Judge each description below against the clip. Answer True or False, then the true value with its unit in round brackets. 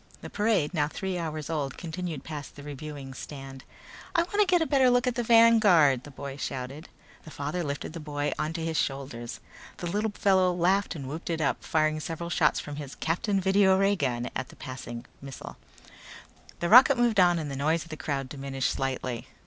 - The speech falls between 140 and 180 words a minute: False (195 wpm)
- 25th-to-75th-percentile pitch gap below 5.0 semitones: False (5.4 semitones)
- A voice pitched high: False (155 Hz)